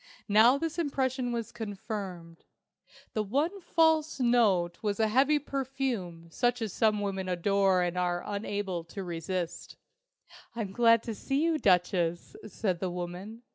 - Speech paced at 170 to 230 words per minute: No, average, 140 wpm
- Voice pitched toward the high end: Yes, high, 210 Hz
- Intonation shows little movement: No, wide, 5.6 semitones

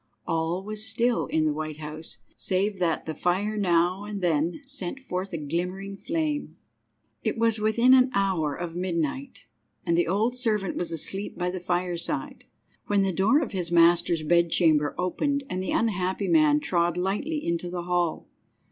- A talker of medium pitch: Yes, medium, 180 Hz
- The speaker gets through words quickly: No, average, 170 wpm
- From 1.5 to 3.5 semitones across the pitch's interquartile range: No, average, 3.9 semitones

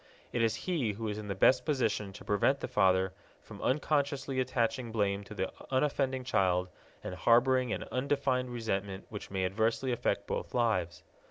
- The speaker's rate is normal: Yes, average, 170 wpm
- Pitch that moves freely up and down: No, average, 4.7 semitones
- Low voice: Yes, low, 115 Hz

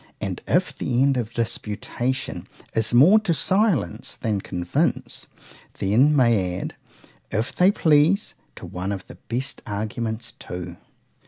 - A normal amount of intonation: No, wide, 6.0 semitones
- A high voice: No, low, 120 Hz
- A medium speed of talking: No, slow, 130 wpm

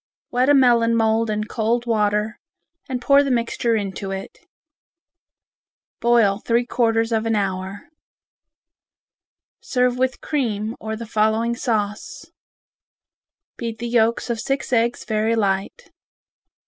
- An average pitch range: No, narrow, 2.0 semitones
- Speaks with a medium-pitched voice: No, high, 230 Hz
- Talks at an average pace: No, slow, 120 wpm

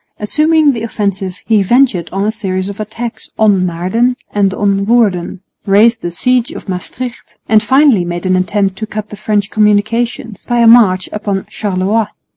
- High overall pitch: Yes, high, 210 Hz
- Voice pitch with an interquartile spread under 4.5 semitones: Yes, average, 3.3 semitones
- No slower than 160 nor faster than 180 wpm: Yes, average, 170 wpm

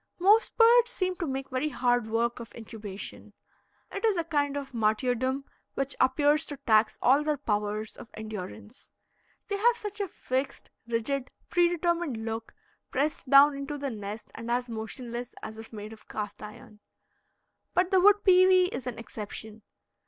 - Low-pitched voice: No, very high, 260 Hz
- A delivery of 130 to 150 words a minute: No, average, 160 wpm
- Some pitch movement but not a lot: No, wide, 6.8 semitones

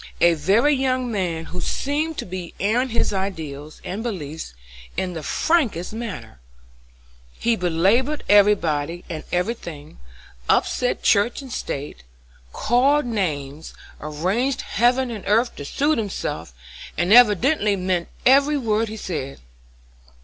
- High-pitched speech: Yes, high, 200 Hz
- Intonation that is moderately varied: No, wide, 6.8 semitones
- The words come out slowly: Yes, slow, 125 wpm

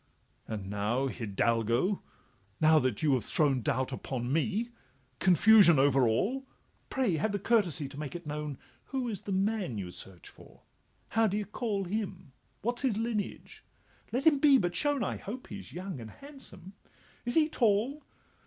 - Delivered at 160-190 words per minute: Yes, average, 170 wpm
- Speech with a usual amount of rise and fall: No, wide, 9.0 semitones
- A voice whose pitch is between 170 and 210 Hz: Yes, medium, 185 Hz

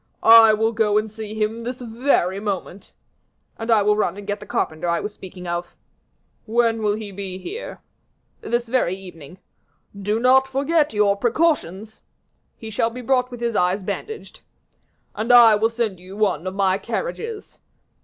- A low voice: No, high, 215 Hz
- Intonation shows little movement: No, average, 3.4 semitones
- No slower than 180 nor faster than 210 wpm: No, average, 170 wpm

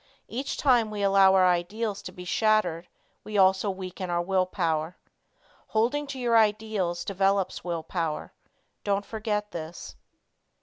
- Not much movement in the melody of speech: No, average, 3.3 semitones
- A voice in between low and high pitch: No, high, 195 Hz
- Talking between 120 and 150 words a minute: Yes, average, 140 wpm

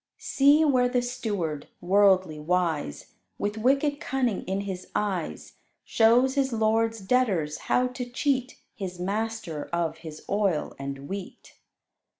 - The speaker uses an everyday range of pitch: No, wide, 6.0 semitones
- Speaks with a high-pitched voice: Yes, high, 205 Hz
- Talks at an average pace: No, slow, 130 wpm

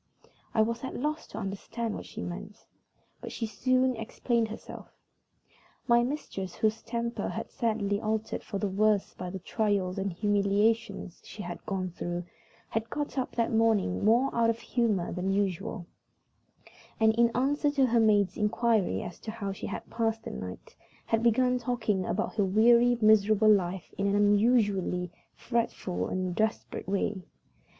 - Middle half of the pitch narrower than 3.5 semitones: Yes, average, 3.0 semitones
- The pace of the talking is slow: No, average, 165 wpm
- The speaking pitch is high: Yes, high, 215 Hz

